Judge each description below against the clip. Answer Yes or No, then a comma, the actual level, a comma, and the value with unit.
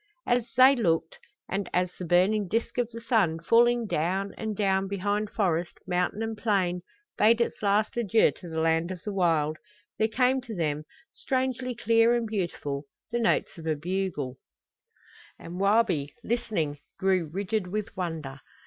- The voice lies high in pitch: Yes, high, 195 Hz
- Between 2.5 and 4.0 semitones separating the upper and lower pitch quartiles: No, average, 4.9 semitones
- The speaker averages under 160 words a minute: No, average, 165 wpm